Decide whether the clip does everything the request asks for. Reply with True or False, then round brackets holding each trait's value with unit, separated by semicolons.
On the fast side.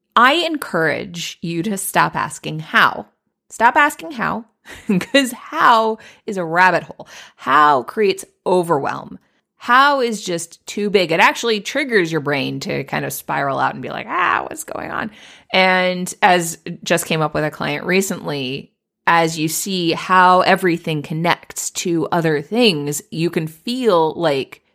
False (155 wpm)